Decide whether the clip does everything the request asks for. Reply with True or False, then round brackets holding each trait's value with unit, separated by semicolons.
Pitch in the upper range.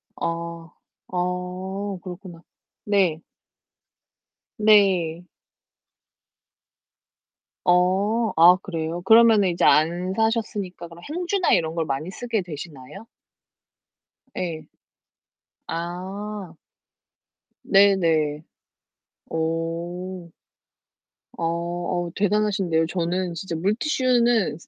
False (180 Hz)